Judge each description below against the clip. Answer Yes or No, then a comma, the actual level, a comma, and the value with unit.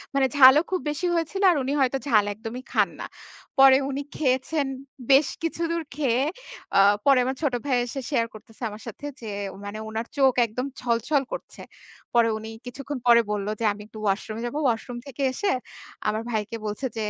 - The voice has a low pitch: No, very high, 255 Hz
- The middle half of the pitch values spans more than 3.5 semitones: Yes, average, 3.9 semitones